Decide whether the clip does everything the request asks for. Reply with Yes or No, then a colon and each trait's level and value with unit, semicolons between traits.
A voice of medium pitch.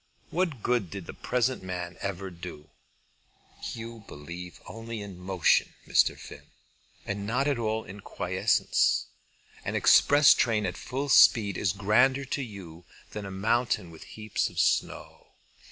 No: low, 105 Hz